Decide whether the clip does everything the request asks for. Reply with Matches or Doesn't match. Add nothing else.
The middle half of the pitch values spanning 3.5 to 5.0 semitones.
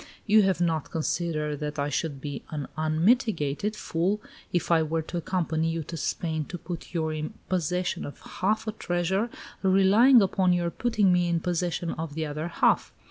Doesn't match